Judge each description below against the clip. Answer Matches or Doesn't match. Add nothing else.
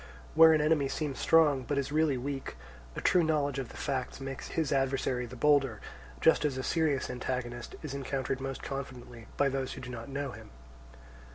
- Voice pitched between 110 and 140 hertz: Matches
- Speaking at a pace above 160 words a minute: Matches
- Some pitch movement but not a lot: Doesn't match